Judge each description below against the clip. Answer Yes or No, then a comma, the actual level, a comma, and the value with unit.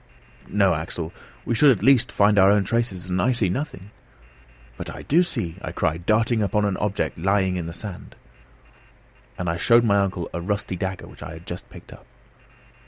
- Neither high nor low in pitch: No, very low, 95 Hz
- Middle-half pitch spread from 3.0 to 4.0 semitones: Yes, average, 3.7 semitones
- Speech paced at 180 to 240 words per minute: Yes, average, 200 wpm